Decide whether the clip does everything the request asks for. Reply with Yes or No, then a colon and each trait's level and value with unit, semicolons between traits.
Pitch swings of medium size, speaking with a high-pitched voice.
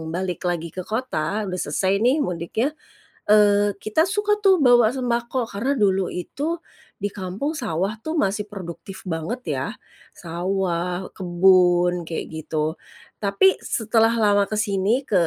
Yes: average, 3.9 semitones; high, 200 Hz